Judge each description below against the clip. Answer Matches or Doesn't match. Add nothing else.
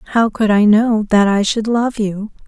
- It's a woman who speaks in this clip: Matches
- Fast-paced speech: Matches